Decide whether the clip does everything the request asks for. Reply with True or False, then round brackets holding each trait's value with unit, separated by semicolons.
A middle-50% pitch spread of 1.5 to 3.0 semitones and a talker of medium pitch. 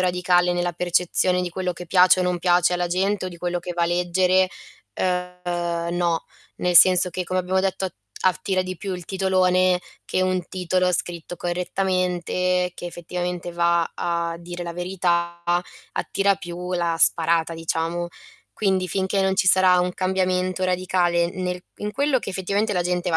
False (1.1 semitones; 180 Hz)